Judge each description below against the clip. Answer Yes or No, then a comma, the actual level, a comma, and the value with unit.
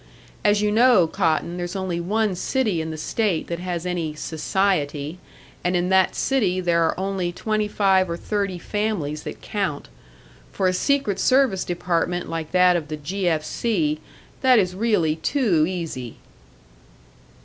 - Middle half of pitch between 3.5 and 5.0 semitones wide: Yes, average, 3.8 semitones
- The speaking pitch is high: No, medium, 180 Hz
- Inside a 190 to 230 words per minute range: No, average, 160 wpm